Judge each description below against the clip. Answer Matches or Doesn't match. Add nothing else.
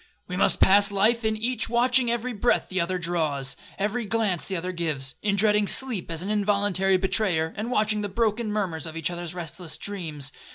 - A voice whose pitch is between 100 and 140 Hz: Doesn't match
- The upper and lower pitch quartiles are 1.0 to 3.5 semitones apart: Doesn't match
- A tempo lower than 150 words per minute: Doesn't match